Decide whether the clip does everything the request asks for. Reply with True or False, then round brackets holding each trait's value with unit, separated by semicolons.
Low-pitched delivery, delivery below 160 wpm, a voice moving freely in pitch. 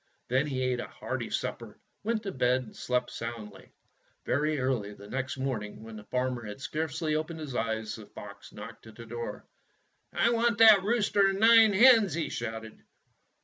False (130 Hz; 185 wpm; 8.8 semitones)